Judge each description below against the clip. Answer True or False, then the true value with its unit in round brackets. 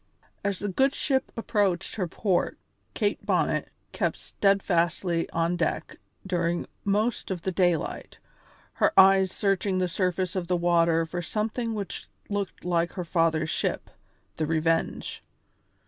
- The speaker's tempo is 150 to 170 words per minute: False (135 wpm)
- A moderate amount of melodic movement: True (3.0 semitones)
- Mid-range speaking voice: True (180 Hz)